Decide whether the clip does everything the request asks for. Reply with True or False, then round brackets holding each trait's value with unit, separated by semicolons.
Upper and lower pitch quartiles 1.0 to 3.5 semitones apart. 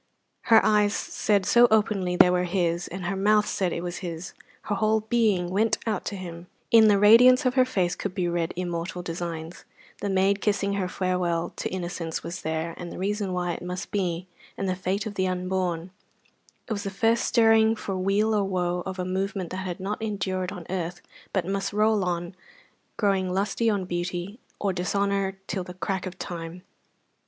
True (2.5 semitones)